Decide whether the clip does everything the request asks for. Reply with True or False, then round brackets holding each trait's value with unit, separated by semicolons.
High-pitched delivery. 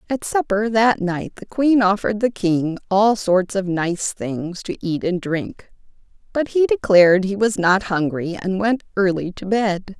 True (200 Hz)